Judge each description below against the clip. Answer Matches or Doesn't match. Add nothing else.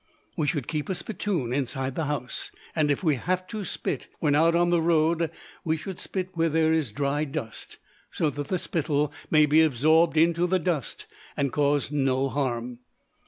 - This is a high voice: Doesn't match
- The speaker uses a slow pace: Doesn't match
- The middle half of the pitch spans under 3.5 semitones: Matches